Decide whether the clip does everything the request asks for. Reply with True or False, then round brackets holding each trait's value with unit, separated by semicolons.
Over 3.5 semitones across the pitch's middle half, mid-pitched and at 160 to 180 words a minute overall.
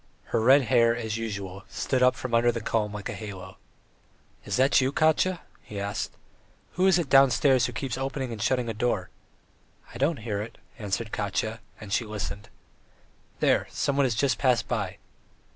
False (3.9 semitones; 115 Hz; 175 wpm)